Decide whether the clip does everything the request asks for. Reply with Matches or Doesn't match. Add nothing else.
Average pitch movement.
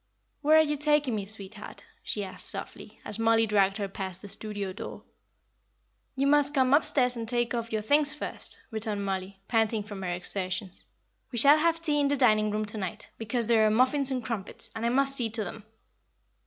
Matches